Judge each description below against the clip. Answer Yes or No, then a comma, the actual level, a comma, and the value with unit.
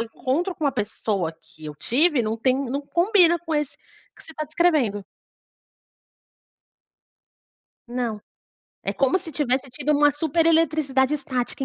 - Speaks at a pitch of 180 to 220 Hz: No, very high, 280 Hz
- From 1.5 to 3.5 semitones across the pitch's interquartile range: No, average, 5.0 semitones